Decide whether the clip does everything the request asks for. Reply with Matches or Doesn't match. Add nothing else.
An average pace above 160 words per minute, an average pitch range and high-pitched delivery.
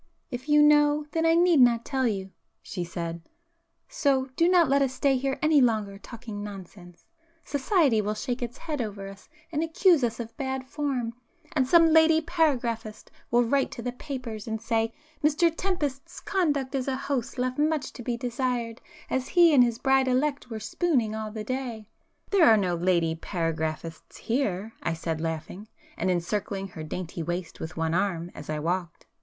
Doesn't match